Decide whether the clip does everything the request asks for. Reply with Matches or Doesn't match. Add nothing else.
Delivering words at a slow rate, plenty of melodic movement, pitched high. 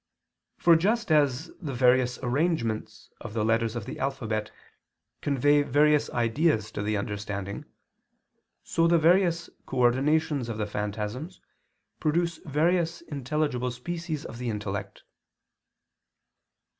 Doesn't match